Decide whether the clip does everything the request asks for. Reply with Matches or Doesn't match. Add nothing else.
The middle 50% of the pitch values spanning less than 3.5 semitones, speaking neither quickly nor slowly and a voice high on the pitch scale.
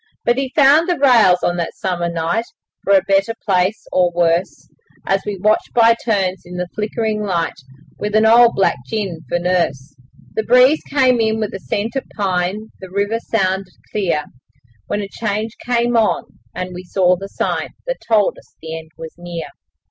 Doesn't match